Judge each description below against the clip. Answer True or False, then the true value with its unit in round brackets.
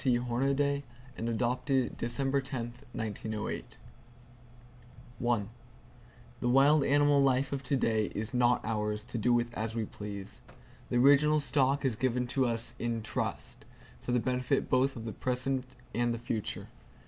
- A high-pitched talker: False (125 Hz)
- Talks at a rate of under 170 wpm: True (150 wpm)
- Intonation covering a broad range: False (2.8 semitones)